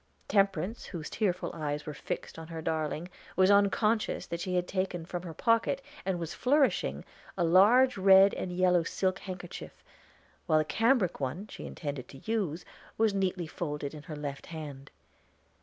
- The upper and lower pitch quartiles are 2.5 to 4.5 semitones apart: Yes, average, 4.0 semitones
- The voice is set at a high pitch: No, medium, 180 Hz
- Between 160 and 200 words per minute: Yes, average, 165 wpm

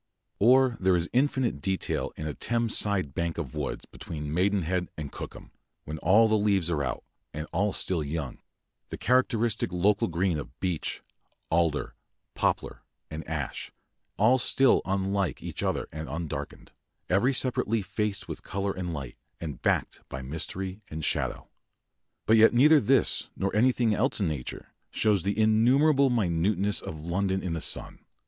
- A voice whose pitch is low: Yes, very low, 95 Hz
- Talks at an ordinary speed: Yes, average, 160 wpm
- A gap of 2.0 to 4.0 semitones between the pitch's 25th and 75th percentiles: No, average, 5.2 semitones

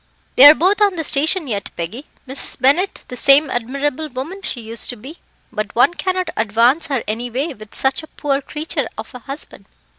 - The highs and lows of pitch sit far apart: No, average, 4.6 semitones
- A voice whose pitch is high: Yes, very high, 275 Hz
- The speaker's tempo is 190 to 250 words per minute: Yes, average, 200 wpm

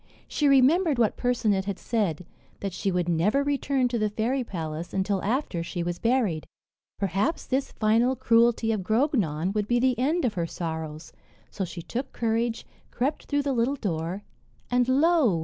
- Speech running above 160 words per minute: Yes, average, 170 wpm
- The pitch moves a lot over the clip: Yes, wide, 6.2 semitones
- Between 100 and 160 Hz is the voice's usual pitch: No, high, 225 Hz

